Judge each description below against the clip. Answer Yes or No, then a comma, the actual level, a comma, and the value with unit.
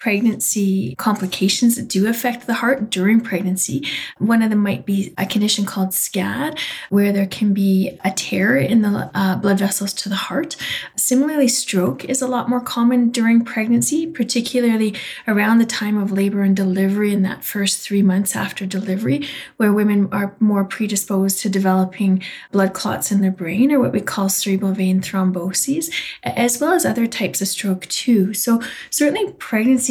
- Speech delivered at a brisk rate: No, average, 175 wpm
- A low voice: No, high, 205 Hz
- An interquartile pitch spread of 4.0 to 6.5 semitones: No, average, 3.4 semitones